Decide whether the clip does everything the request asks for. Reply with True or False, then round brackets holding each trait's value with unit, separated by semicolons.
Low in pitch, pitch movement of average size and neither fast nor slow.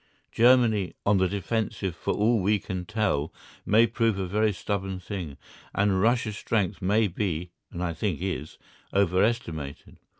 True (100 Hz; 3.3 semitones; 145 wpm)